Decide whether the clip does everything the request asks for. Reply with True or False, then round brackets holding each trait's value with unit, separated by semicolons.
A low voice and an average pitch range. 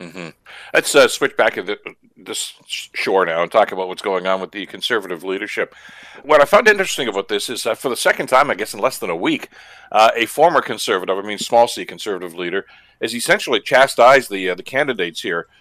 True (95 Hz; 4.4 semitones)